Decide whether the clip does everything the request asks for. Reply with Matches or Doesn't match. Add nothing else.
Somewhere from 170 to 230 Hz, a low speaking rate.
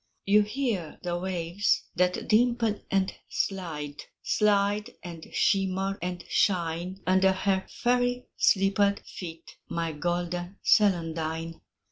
Matches